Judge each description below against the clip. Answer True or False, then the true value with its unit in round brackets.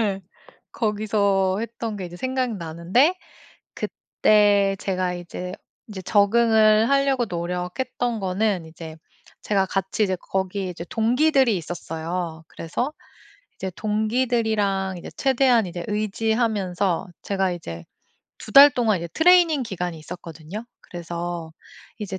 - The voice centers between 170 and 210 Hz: True (200 Hz)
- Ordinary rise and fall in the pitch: True (4.2 semitones)